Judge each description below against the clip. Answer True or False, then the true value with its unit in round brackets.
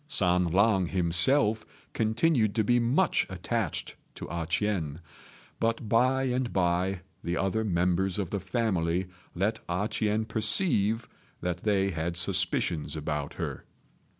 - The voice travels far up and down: False (4.2 semitones)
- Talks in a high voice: False (100 Hz)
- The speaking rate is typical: False (130 wpm)